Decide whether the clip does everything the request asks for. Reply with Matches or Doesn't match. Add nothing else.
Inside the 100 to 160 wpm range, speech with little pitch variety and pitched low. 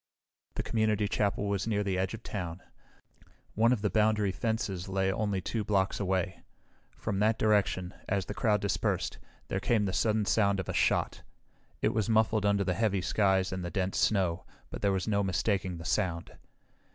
Doesn't match